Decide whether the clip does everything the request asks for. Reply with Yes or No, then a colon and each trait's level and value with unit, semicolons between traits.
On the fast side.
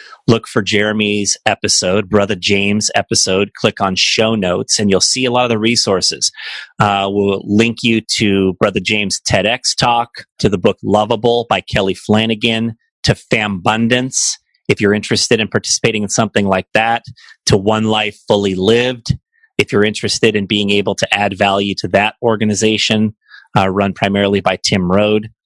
No: average, 165 wpm